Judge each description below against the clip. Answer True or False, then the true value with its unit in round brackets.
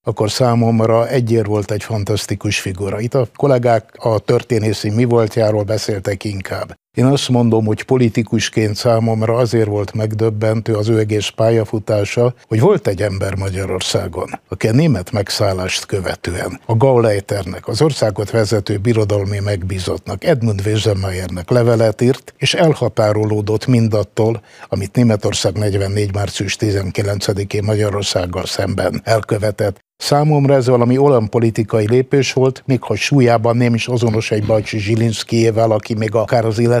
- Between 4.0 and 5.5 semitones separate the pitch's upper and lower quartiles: False (2.4 semitones)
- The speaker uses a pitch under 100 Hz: False (110 Hz)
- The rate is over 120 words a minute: True (135 wpm)